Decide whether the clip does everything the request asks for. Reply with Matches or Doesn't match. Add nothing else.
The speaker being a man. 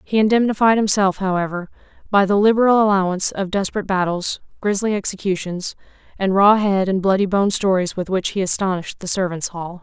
Doesn't match